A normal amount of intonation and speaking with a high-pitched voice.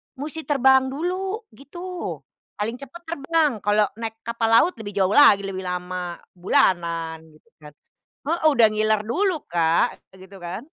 No: wide, 7.8 semitones; high, 225 Hz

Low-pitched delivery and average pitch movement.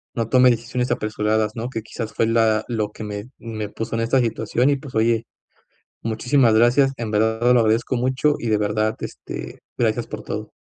No: low, 115 Hz; narrow, 2.1 semitones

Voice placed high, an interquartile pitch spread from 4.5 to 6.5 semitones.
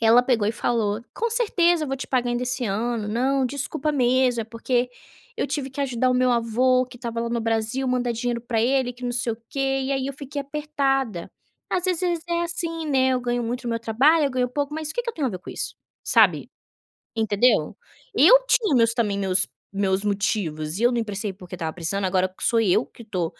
No: high, 245 Hz; average, 3.6 semitones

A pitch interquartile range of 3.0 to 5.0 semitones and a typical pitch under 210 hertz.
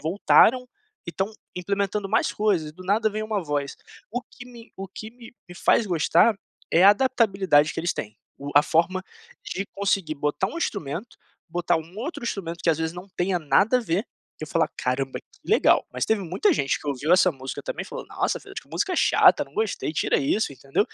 No: wide, 5.4 semitones; medium, 185 Hz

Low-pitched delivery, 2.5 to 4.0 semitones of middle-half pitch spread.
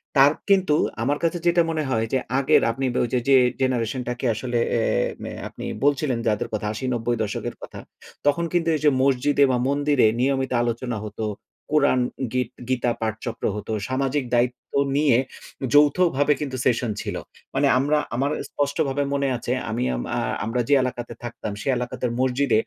Yes: low, 130 Hz; average, 3.1 semitones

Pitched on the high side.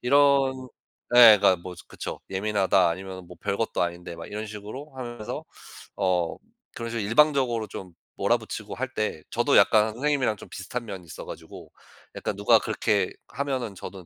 No: low, 105 Hz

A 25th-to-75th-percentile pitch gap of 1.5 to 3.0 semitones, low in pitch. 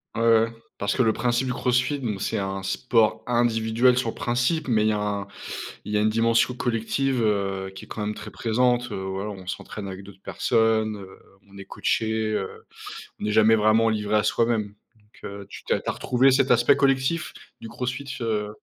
Yes: average, 2.7 semitones; low, 110 Hz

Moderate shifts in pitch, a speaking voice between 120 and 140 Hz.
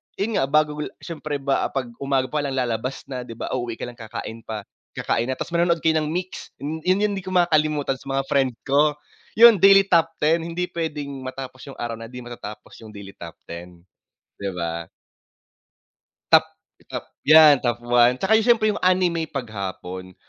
No: wide, 5.7 semitones; low, 135 Hz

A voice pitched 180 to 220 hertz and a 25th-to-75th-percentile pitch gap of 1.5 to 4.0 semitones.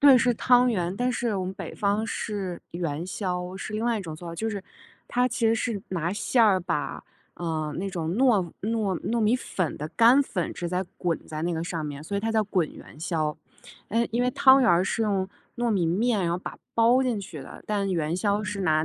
No: high, 195 Hz; average, 5.0 semitones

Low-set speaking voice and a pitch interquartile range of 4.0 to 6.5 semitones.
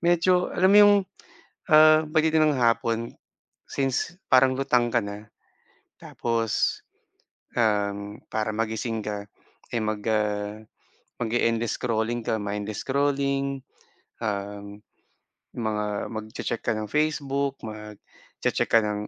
Yes: low, 115 Hz; average, 4.4 semitones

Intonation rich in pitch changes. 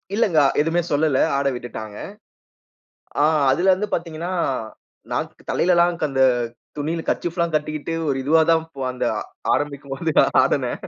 No: average, 3.2 semitones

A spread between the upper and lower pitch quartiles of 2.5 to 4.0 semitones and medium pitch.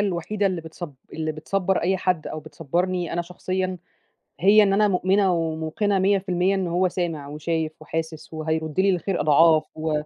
Yes: average, 3.0 semitones; medium, 175 Hz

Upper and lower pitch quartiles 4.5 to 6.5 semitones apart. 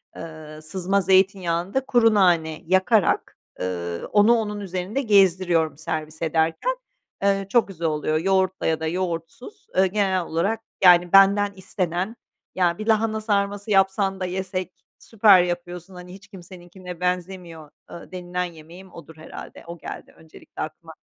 No: average, 3.0 semitones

